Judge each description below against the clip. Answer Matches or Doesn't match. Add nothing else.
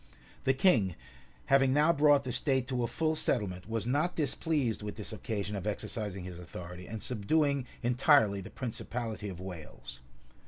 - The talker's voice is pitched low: Matches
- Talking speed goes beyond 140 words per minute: Matches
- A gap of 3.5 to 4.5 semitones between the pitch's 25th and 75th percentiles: Doesn't match